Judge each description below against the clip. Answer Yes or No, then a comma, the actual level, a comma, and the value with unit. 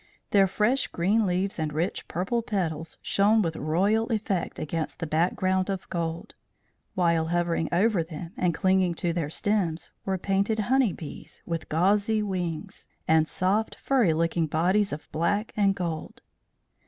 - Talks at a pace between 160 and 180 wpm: No, average, 150 wpm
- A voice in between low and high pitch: Yes, medium, 180 Hz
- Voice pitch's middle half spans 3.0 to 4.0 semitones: Yes, average, 3.7 semitones